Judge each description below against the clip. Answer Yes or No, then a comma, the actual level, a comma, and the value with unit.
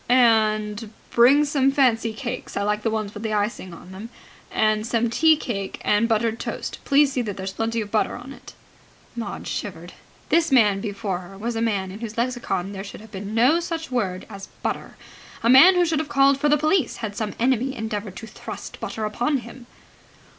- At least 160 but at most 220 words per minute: Yes, average, 195 wpm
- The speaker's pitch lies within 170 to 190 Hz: No, high, 225 Hz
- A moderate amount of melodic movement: Yes, average, 3.9 semitones